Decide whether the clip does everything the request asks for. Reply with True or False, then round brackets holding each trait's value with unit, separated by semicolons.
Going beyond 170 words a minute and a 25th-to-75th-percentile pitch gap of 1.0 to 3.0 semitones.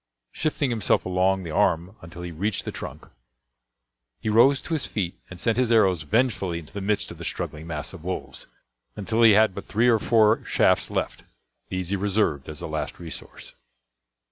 False (190 wpm; 4.3 semitones)